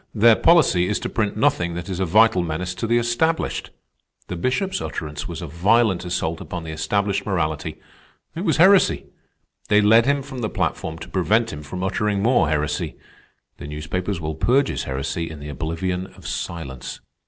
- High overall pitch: No, very low, 95 Hz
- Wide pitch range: Yes, wide, 5.9 semitones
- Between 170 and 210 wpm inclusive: Yes, average, 180 wpm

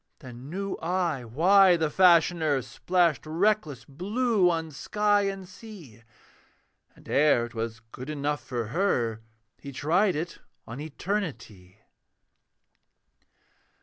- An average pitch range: No, wide, 6.6 semitones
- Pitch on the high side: No, medium, 160 Hz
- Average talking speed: No, slow, 110 wpm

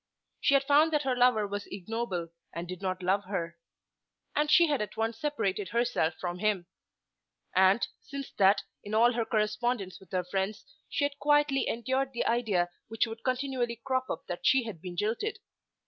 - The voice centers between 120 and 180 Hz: No, high, 225 Hz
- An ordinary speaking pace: Yes, average, 180 wpm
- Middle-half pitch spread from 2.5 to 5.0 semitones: No, wide, 5.5 semitones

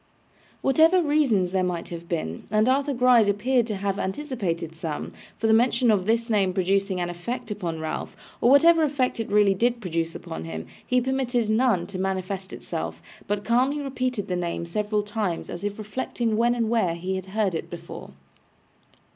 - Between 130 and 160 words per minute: No, average, 180 wpm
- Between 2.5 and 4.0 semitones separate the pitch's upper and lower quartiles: No, average, 5.1 semitones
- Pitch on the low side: No, high, 210 Hz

